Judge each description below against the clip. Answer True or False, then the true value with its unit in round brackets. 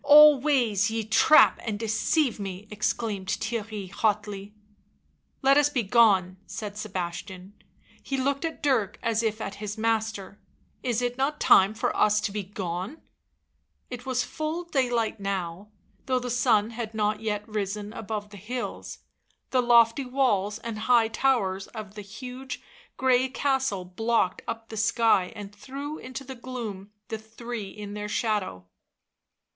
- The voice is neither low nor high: False (220 Hz)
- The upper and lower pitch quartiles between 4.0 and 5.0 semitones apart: False (3.5 semitones)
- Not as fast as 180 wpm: True (155 wpm)